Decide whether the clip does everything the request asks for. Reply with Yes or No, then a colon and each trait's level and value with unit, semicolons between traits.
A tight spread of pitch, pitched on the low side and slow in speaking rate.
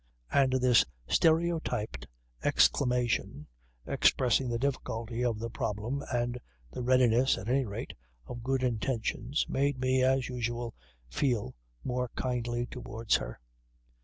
Yes: narrow, 2.0 semitones; low, 125 Hz; slow, 120 wpm